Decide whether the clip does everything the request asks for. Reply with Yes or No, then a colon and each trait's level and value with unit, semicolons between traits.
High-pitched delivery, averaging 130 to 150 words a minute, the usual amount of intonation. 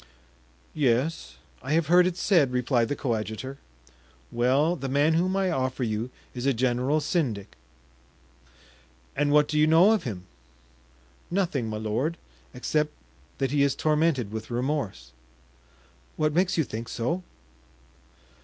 No: medium, 140 Hz; slow, 135 wpm; average, 4.8 semitones